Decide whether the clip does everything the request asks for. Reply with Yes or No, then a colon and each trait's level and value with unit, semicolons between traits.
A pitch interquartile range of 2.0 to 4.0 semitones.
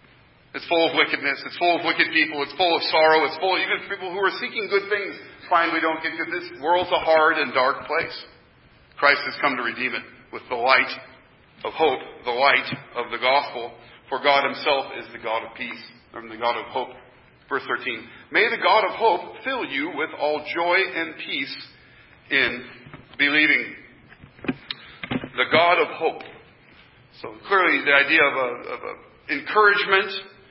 No: average, 4.6 semitones